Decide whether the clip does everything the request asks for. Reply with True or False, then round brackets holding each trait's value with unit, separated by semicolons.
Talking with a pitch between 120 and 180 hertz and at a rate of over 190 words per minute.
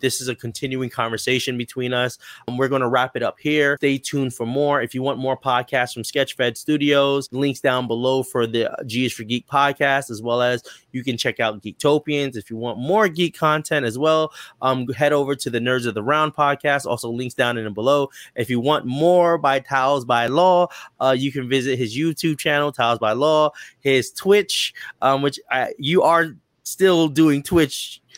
True (135 Hz; 205 wpm)